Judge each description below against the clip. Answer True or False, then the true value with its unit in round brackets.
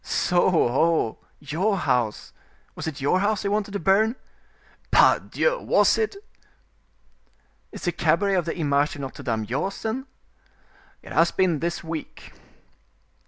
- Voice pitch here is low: False (170 Hz)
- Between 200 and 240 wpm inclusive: False (135 wpm)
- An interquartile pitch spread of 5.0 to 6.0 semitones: True (5.4 semitones)